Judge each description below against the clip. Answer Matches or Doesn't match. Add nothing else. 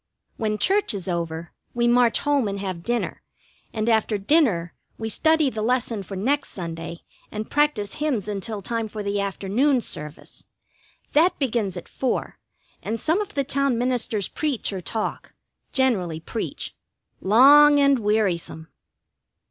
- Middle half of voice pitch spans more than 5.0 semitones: Matches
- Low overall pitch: Doesn't match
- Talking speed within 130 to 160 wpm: Matches